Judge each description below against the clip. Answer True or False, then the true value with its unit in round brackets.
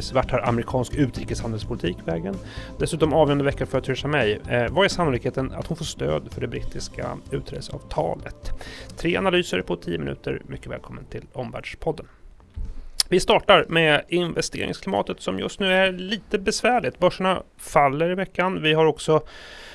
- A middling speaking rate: True (150 wpm)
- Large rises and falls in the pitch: True (7.0 semitones)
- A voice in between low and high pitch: True (145 Hz)